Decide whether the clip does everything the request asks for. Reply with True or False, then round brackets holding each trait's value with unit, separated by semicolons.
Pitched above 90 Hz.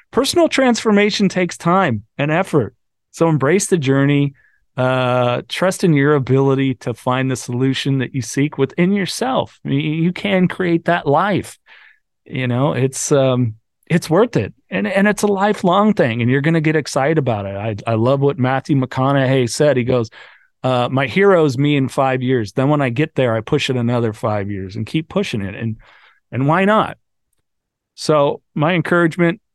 True (140 Hz)